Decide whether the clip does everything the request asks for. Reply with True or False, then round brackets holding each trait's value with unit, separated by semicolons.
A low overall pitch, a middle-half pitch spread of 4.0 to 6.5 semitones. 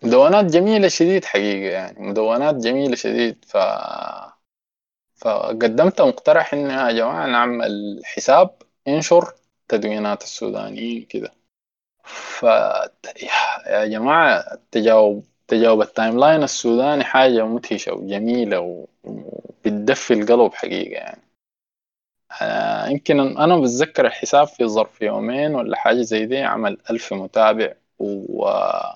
True (120 Hz; 4.6 semitones)